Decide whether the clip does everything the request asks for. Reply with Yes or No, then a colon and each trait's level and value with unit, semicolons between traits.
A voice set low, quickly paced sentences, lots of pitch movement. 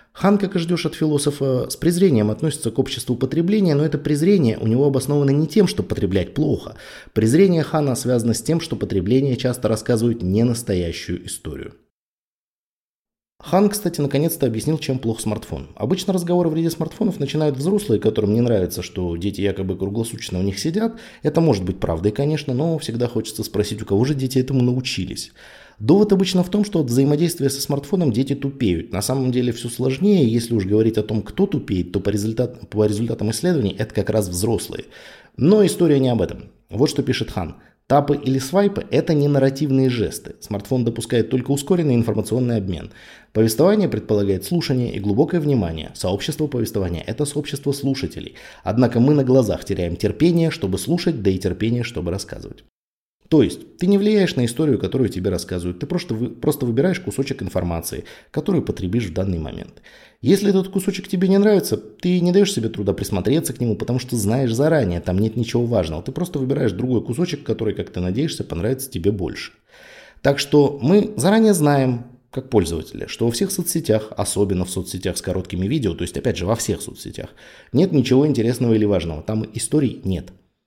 Yes: low, 125 Hz; fast, 180 wpm; wide, 6.4 semitones